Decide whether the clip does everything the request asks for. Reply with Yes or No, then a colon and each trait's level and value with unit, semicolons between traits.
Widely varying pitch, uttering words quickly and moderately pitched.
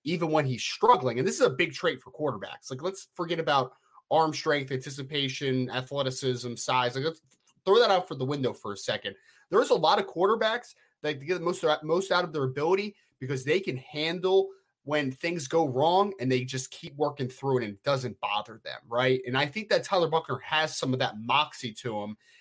No: average, 4.9 semitones; fast, 215 wpm; medium, 150 Hz